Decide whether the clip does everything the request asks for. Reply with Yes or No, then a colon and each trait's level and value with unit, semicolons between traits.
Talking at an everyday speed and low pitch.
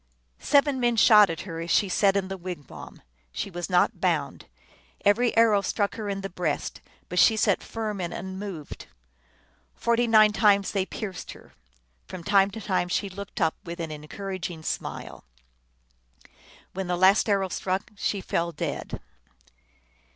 No: average, 160 wpm; high, 195 Hz